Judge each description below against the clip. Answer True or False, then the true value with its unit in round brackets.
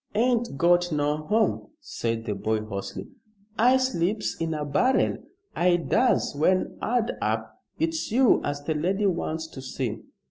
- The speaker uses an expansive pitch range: True (7.8 semitones)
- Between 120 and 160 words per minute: True (150 wpm)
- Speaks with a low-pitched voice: False (170 Hz)